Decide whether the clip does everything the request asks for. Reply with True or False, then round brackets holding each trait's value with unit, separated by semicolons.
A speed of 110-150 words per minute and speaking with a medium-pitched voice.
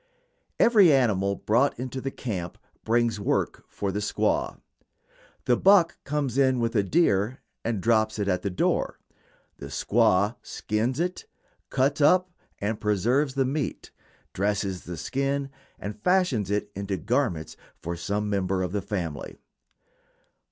False (140 wpm; 110 Hz)